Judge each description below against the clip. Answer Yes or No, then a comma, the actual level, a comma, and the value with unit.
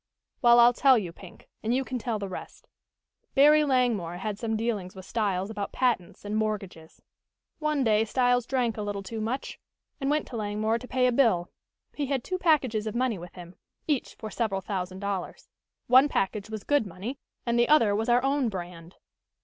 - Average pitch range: Yes, average, 4.3 semitones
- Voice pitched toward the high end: Yes, high, 225 Hz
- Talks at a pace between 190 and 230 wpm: Yes, average, 195 wpm